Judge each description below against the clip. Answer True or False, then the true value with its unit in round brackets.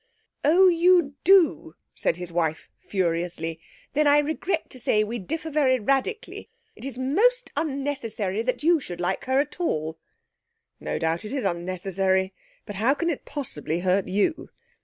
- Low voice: False (250 Hz)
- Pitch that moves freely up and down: True (8.6 semitones)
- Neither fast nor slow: True (160 wpm)